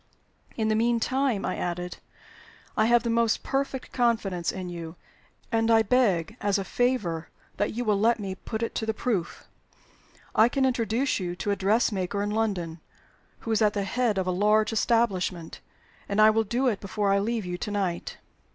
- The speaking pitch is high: Yes, high, 215 Hz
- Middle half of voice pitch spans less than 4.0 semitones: Yes, average, 3.5 semitones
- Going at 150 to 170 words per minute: No, average, 190 wpm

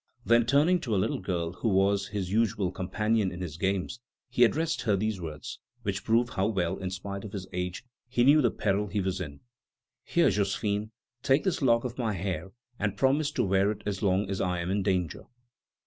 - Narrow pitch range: No, average, 3.6 semitones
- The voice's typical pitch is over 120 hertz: No, low, 100 Hz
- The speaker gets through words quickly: Yes, fast, 210 wpm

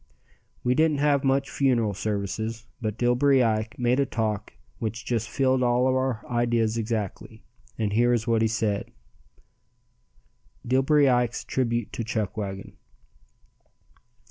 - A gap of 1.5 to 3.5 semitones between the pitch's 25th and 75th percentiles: Yes, average, 2.8 semitones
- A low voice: Yes, low, 120 Hz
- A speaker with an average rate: No, slow, 125 wpm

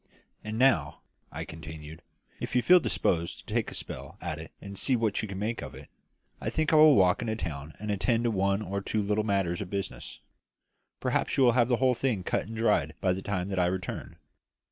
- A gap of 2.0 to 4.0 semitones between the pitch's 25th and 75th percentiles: No, average, 4.4 semitones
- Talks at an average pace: No, fast, 230 wpm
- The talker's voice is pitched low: Yes, low, 100 Hz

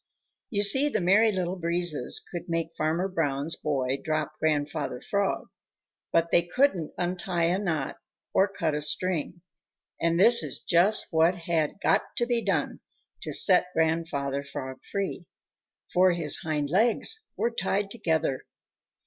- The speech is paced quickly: No, average, 145 wpm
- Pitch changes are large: No, average, 3.8 semitones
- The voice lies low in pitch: No, medium, 170 Hz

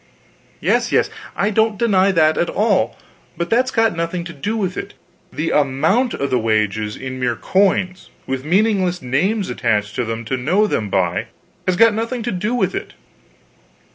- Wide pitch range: Yes, wide, 8.4 semitones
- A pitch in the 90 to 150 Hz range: No, medium, 175 Hz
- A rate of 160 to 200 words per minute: Yes, average, 175 wpm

